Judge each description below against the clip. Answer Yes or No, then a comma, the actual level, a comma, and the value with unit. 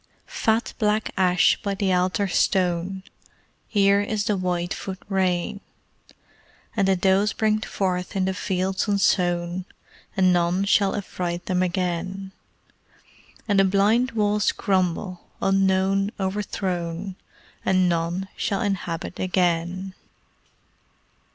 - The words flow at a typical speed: No, slow, 110 wpm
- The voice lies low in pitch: No, high, 190 Hz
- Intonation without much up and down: Yes, narrow, 1.8 semitones